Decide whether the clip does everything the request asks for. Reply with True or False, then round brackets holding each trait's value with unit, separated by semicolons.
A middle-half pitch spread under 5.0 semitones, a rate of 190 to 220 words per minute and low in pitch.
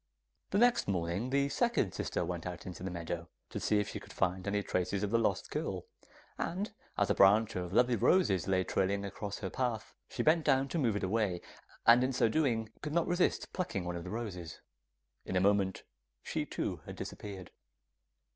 False (5.5 semitones; 200 wpm; 105 Hz)